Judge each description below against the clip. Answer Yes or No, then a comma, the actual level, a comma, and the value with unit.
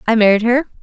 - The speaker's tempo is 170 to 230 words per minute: Yes, fast, 220 wpm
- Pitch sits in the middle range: No, high, 230 Hz